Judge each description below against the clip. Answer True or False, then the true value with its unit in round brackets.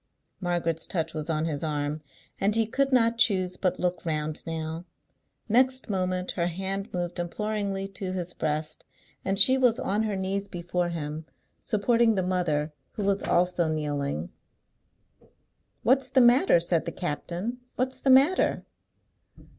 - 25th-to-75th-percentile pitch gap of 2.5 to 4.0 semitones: False (4.8 semitones)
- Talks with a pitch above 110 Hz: True (185 Hz)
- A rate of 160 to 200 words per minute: False (145 wpm)